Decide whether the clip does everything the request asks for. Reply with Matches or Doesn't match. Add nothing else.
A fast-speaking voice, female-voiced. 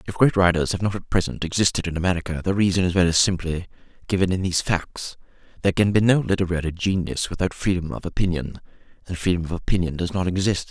Doesn't match